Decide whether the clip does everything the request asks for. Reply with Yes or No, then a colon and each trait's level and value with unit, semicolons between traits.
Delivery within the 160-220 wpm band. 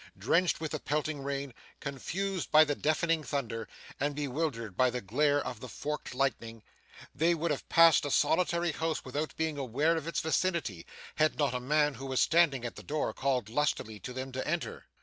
Yes: average, 190 wpm